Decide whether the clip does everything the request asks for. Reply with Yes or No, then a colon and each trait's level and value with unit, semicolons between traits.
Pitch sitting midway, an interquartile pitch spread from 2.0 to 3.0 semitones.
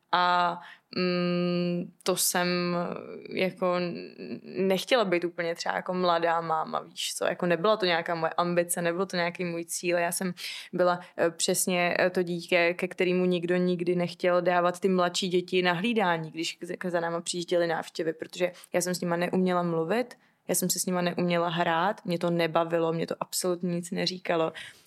No: medium, 175 Hz; narrow, 1.0 semitones